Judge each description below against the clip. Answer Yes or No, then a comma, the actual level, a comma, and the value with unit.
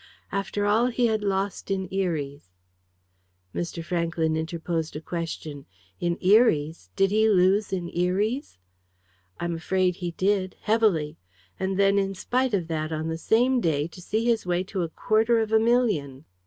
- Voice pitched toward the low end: No, medium, 185 Hz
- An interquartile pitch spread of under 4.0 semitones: No, average, 4.5 semitones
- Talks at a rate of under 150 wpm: No, average, 170 wpm